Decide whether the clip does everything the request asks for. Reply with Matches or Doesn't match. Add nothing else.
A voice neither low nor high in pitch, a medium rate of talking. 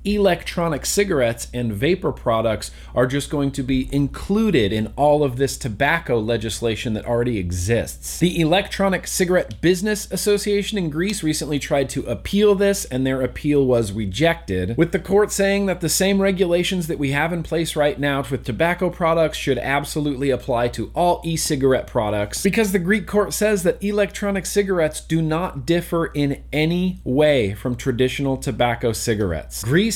Matches